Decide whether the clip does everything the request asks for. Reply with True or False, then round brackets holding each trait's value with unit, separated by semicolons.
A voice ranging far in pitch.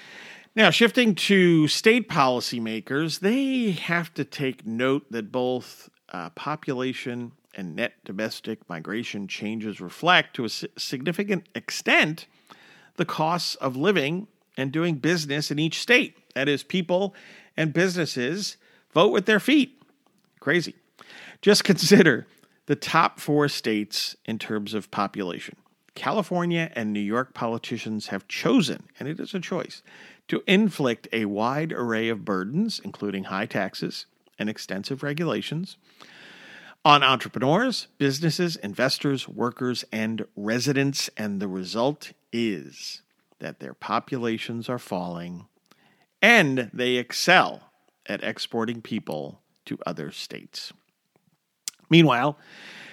True (7.8 semitones)